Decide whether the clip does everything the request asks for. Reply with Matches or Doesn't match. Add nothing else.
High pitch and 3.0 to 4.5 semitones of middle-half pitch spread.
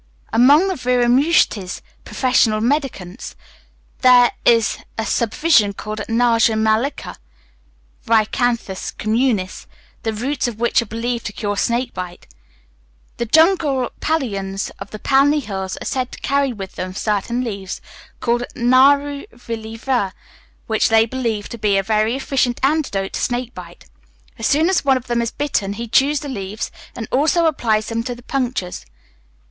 Matches